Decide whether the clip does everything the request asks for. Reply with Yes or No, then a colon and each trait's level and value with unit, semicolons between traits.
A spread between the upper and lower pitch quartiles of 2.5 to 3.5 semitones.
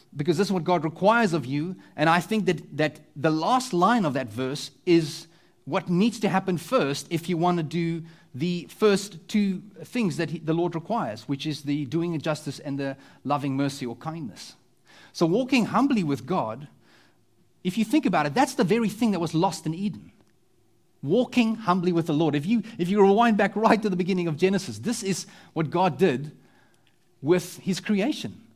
No: average, 4.3 semitones